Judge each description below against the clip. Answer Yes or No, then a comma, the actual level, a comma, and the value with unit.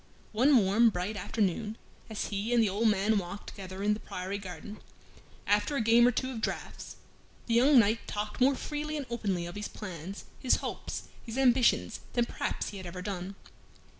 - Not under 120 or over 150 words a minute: No, average, 190 wpm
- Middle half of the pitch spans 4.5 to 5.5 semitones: No, average, 3.4 semitones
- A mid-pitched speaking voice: No, high, 210 Hz